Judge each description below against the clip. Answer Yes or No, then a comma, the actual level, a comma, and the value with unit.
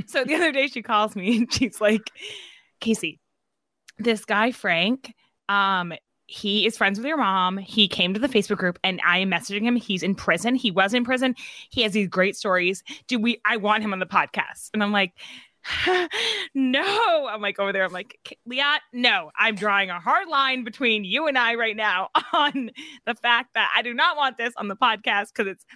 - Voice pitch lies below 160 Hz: No, high, 225 Hz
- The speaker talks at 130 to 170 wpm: No, fast, 205 wpm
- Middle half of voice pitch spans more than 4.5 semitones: Yes, average, 5.0 semitones